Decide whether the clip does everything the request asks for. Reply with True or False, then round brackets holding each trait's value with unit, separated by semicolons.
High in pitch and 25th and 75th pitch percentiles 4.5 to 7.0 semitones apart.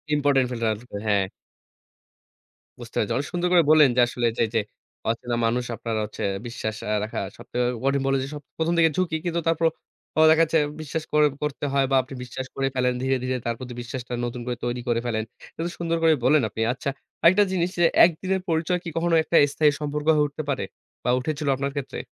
False (140 Hz; 4.8 semitones)